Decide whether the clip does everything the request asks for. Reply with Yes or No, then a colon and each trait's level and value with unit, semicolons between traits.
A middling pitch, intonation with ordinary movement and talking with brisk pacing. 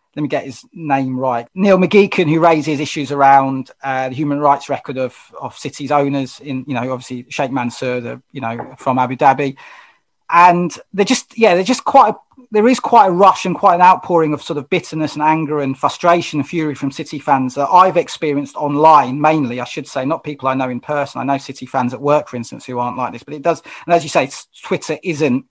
Yes: medium, 145 Hz; average, 4.2 semitones; fast, 235 wpm